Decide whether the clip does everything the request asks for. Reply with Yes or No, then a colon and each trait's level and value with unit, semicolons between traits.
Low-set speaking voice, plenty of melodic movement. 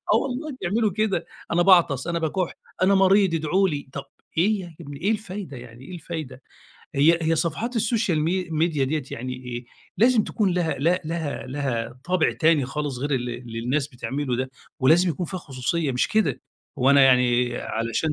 No: medium, 155 Hz; wide, 5.8 semitones